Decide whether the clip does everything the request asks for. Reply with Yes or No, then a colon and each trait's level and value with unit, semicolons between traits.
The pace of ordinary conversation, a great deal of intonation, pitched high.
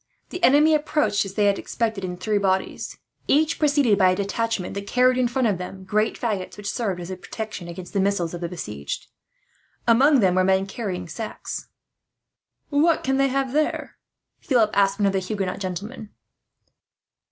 No: average, 180 wpm; average, 5.0 semitones; high, 205 Hz